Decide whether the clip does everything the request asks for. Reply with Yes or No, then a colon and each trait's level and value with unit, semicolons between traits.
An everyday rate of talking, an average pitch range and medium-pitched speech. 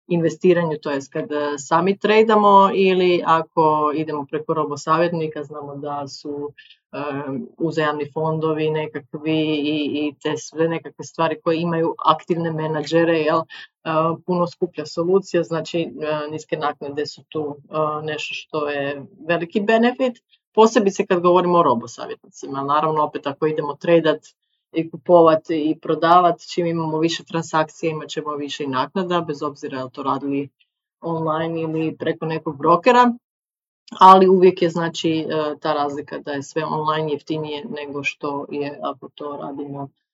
No: average, 140 wpm; narrow, 2.3 semitones; medium, 155 Hz